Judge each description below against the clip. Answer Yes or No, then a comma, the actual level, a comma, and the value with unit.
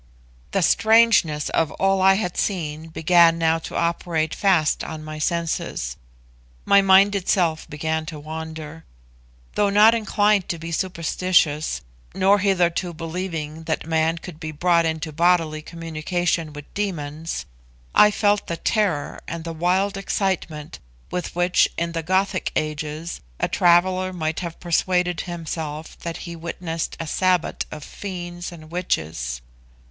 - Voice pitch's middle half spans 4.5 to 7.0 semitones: No, average, 2.7 semitones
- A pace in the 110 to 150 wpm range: Yes, average, 140 wpm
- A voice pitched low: No, medium, 170 Hz